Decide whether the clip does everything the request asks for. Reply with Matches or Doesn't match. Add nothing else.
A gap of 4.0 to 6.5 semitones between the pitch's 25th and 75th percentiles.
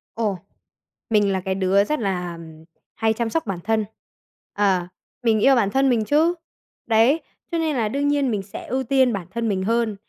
Matches